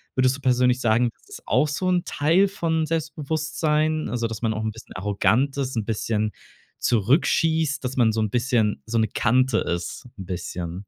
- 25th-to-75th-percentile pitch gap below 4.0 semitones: No, wide, 5.6 semitones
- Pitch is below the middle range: Yes, low, 125 Hz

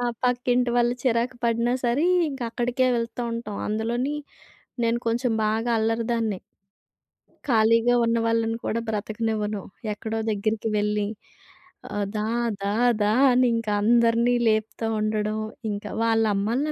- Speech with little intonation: Yes, narrow, 1.9 semitones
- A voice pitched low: No, high, 230 Hz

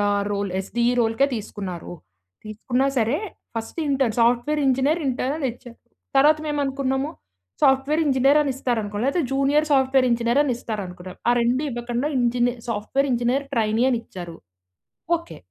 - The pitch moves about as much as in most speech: Yes, average, 3.5 semitones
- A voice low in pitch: No, high, 245 Hz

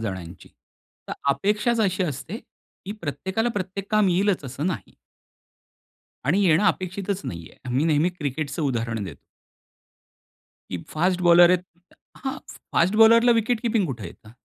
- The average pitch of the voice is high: No, medium, 180 Hz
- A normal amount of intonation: No, wide, 6.4 semitones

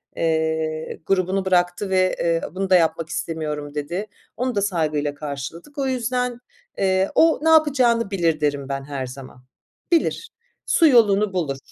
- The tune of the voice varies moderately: No, wide, 5.8 semitones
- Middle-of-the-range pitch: Yes, medium, 175 Hz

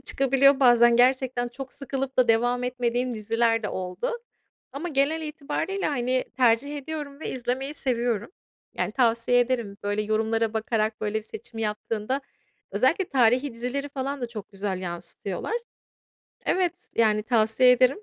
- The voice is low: No, high, 245 Hz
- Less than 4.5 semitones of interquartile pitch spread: Yes, average, 3.4 semitones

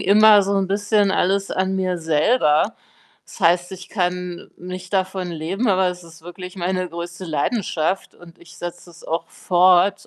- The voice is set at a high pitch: No, medium, 180 Hz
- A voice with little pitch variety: Yes, narrow, 1.9 semitones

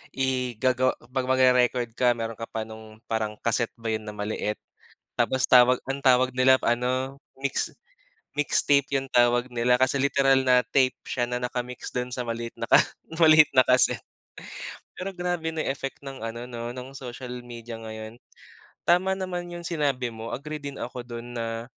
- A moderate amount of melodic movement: No, narrow, 2.3 semitones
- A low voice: Yes, low, 125 Hz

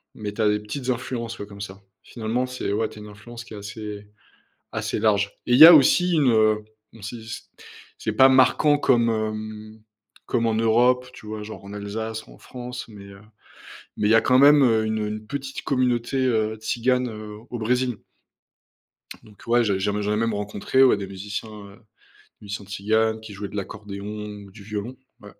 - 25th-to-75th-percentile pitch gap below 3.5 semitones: Yes, average, 2.8 semitones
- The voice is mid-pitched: No, low, 110 Hz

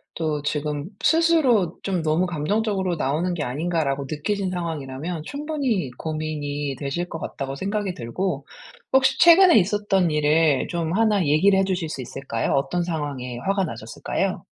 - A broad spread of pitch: No, average, 5.0 semitones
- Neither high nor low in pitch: Yes, medium, 165 Hz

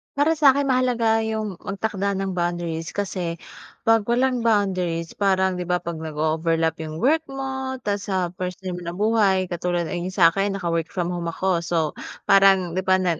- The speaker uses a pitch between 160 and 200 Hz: Yes, high, 190 Hz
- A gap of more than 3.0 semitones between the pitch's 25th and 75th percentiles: Yes, average, 4.2 semitones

